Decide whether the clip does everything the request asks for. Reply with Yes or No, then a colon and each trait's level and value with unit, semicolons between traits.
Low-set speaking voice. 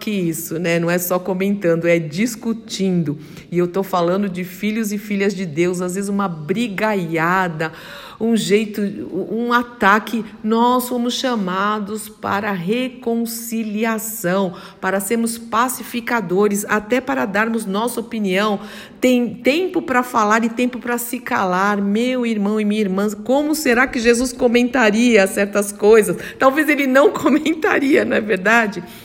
No: high, 215 Hz